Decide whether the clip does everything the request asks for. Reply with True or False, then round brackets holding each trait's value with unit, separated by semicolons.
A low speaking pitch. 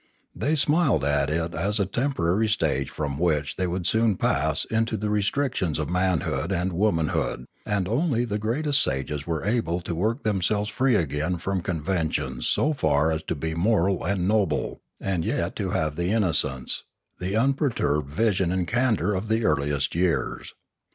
True (90 Hz)